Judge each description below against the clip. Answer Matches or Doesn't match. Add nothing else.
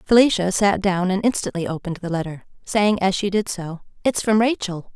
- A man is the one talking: Doesn't match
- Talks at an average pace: Matches